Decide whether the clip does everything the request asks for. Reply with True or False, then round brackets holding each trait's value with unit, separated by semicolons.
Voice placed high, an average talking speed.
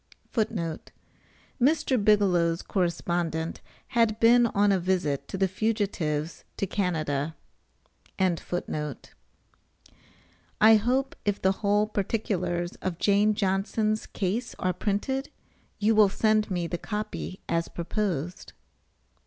False (195 Hz; 110 wpm)